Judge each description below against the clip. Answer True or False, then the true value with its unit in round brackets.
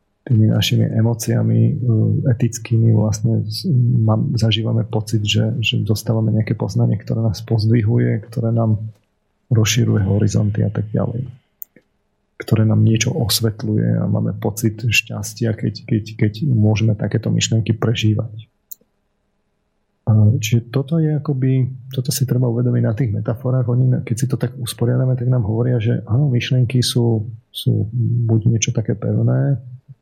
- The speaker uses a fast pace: False (130 wpm)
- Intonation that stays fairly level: True (2.1 semitones)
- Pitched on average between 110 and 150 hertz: True (115 Hz)